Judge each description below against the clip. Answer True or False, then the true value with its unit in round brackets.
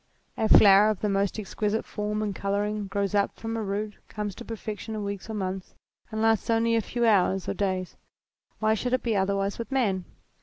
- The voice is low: False (210 Hz)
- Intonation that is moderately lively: False (1.8 semitones)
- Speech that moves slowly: False (205 wpm)